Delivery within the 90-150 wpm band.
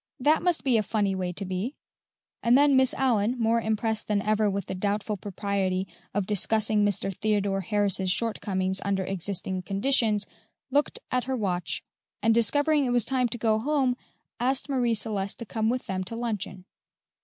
No: average, 175 wpm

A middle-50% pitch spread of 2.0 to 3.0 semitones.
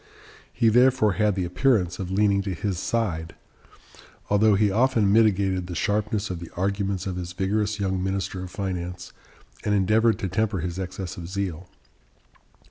Yes: average, 2.7 semitones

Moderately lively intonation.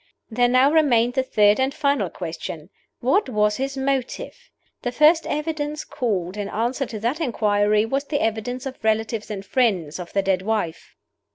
Yes: average, 4.6 semitones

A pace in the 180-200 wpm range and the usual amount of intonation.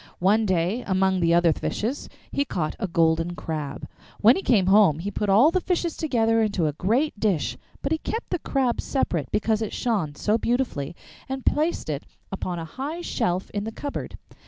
No: average, 190 wpm; wide, 7.0 semitones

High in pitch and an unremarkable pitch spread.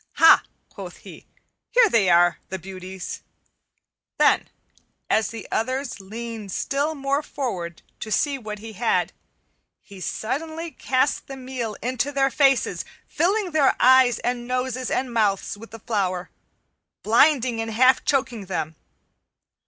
Yes: high, 240 Hz; average, 4.5 semitones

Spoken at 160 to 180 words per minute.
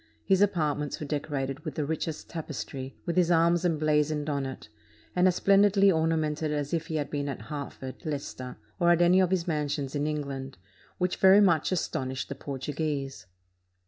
Yes: average, 175 wpm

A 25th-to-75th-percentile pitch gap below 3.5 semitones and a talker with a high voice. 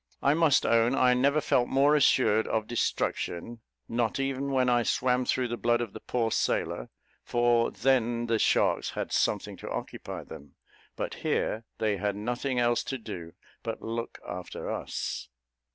No: narrow, 2.5 semitones; low, 120 Hz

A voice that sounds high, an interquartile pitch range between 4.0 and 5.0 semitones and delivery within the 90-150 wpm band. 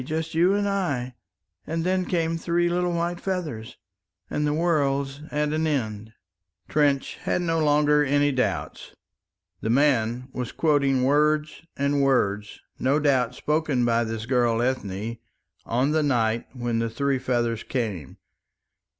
No: medium, 140 Hz; average, 4.6 semitones; average, 140 wpm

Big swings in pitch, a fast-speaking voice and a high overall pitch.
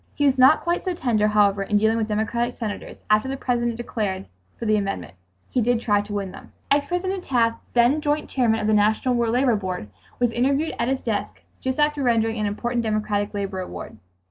No: average, 3.8 semitones; fast, 210 wpm; high, 230 Hz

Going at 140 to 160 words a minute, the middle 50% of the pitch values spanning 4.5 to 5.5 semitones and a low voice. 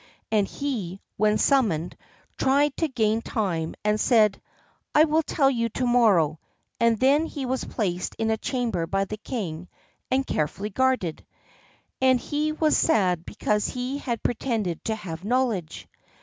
No: average, 150 wpm; average, 5.1 semitones; high, 225 Hz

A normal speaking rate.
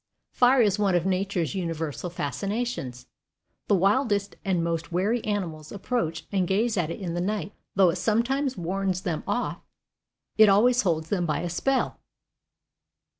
Yes: average, 160 wpm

